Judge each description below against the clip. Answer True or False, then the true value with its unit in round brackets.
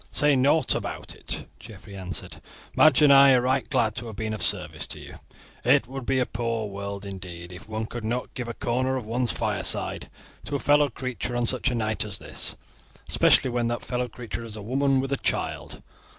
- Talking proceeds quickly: True (210 wpm)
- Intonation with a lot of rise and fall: False (3.3 semitones)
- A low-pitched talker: True (120 Hz)